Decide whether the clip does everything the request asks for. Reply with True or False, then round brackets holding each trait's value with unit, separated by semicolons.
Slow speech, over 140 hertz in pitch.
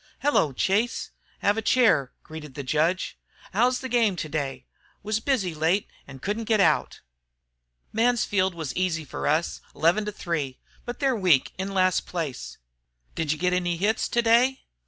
False (155 wpm; 185 Hz)